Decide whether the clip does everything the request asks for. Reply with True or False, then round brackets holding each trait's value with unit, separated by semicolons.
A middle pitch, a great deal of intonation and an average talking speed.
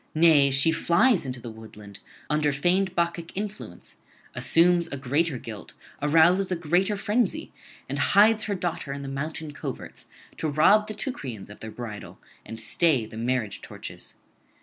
True (155 Hz; 5.9 semitones; 155 wpm)